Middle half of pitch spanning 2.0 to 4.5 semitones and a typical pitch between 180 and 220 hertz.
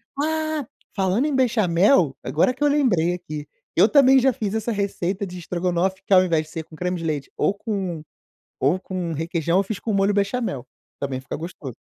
No: average, 4.9 semitones; medium, 185 Hz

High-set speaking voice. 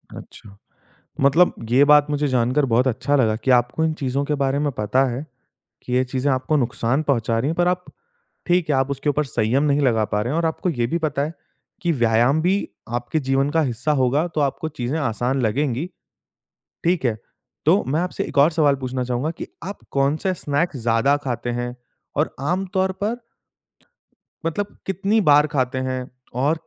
No: medium, 140 Hz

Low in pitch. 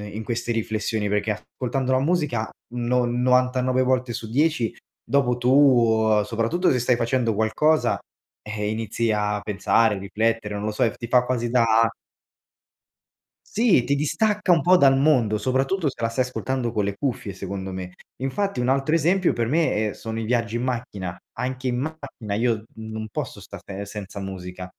Yes: low, 120 Hz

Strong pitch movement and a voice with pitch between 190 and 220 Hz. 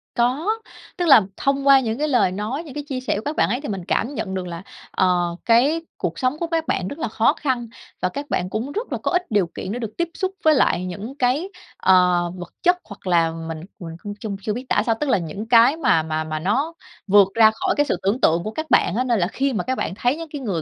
No: wide, 7.2 semitones; high, 230 Hz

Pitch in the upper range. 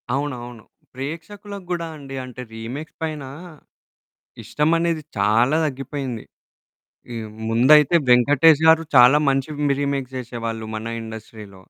No: low, 135 Hz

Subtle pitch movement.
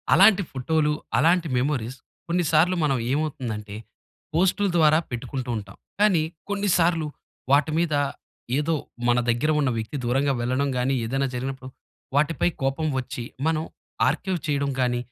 No: average, 4.2 semitones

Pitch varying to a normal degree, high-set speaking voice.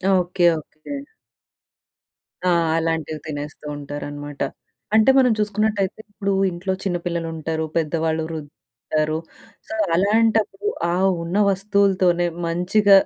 No: average, 4.1 semitones; medium, 175 Hz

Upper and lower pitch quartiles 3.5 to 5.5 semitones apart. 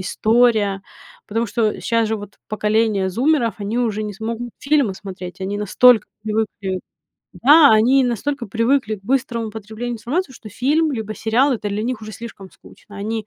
No: average, 2.9 semitones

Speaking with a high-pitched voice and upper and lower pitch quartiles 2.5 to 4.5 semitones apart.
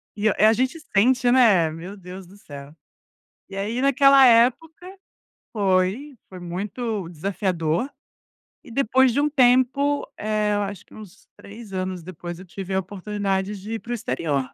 No: high, 205 Hz; average, 4.9 semitones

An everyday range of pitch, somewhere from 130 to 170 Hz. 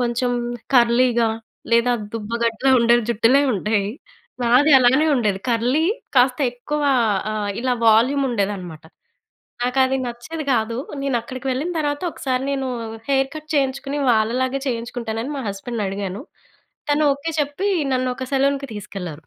No: average, 3.2 semitones; high, 245 Hz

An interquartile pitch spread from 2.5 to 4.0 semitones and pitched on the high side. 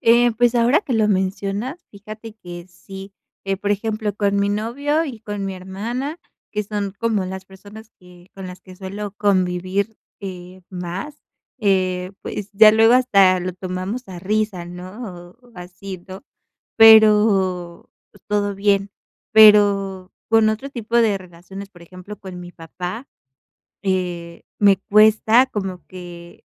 Yes: average, 2.9 semitones; high, 200 Hz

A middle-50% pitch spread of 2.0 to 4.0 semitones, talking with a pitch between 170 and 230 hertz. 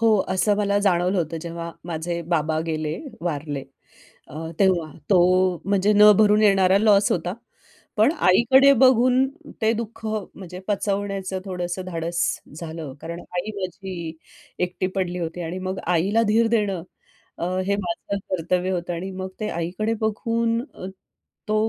Yes: average, 3.5 semitones; medium, 185 Hz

